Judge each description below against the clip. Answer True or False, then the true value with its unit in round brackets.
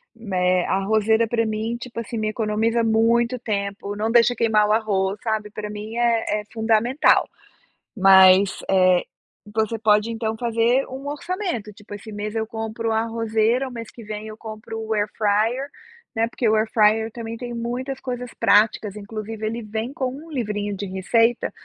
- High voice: True (220 Hz)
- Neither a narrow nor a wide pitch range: False (1.8 semitones)